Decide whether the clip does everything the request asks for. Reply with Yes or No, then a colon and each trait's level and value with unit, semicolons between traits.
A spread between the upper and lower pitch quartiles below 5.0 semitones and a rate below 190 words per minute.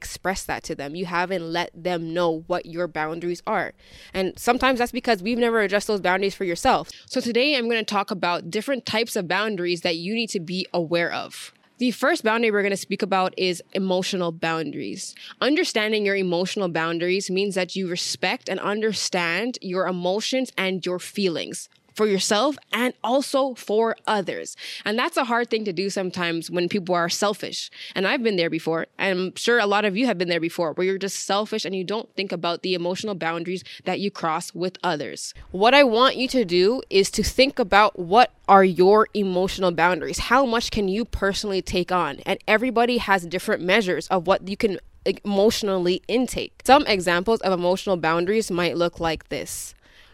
No: average, 3.7 semitones; average, 195 wpm